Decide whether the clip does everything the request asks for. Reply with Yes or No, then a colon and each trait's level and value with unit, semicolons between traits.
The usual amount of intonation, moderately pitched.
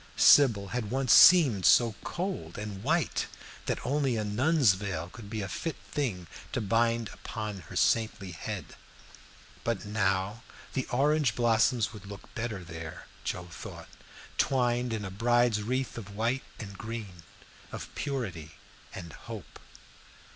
No: average, 3.8 semitones; low, 110 Hz